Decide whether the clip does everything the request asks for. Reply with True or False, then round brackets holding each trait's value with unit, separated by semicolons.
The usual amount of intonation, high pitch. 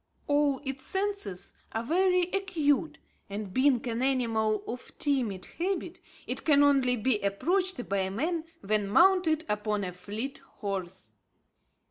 False (7.3 semitones; 260 Hz)